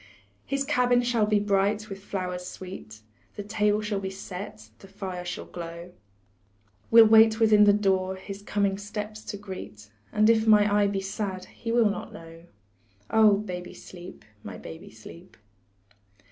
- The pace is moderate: Yes, average, 160 wpm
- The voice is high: Yes, high, 200 Hz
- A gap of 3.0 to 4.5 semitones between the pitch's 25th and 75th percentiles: No, narrow, 2.5 semitones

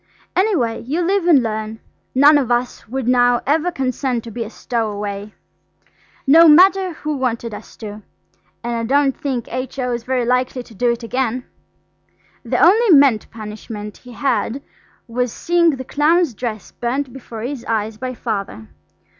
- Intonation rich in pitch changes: No, average, 3.9 semitones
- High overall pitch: Yes, very high, 250 Hz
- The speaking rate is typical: Yes, average, 160 wpm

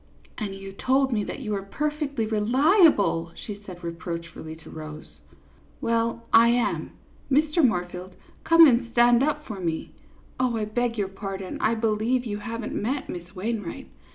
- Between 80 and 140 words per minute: No, average, 175 wpm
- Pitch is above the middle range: Yes, high, 220 Hz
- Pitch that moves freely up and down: No, average, 4.6 semitones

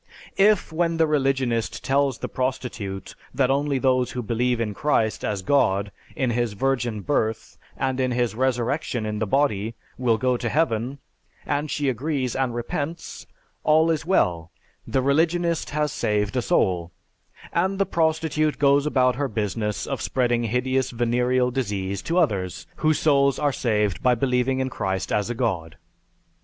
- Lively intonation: No, average, 4.2 semitones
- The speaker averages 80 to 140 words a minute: No, average, 160 wpm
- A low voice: Yes, low, 125 Hz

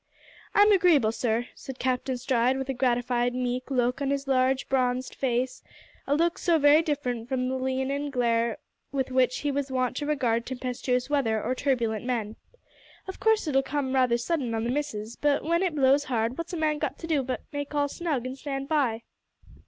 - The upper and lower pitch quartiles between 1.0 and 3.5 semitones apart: Yes, average, 2.8 semitones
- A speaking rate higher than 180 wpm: Yes, average, 195 wpm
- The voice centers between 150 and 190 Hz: No, very high, 260 Hz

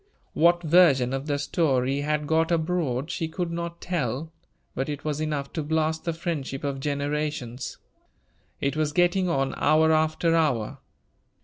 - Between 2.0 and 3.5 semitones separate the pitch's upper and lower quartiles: Yes, average, 3.0 semitones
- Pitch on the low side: No, medium, 155 Hz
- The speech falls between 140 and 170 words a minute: Yes, average, 150 wpm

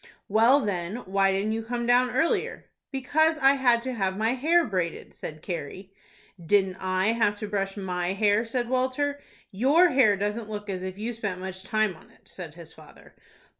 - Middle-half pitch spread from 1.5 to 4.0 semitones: No, average, 4.7 semitones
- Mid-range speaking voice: No, high, 210 Hz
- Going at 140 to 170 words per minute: No, average, 190 wpm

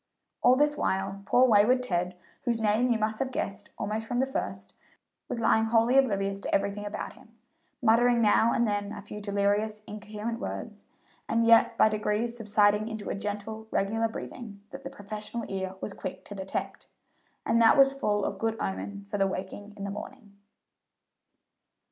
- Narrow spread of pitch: Yes, narrow, 2.3 semitones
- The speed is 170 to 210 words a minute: Yes, average, 175 wpm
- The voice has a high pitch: Yes, high, 215 Hz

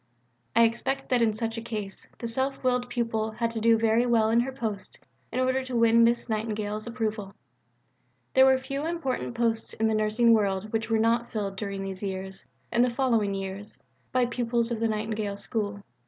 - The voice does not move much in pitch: Yes, narrow, 2.1 semitones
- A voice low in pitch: No, high, 230 Hz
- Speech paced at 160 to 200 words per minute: Yes, average, 190 wpm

